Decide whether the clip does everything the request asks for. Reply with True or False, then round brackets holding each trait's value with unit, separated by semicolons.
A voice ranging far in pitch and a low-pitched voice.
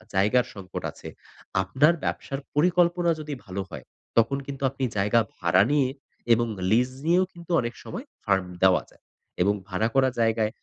True (6.7 semitones; 120 Hz)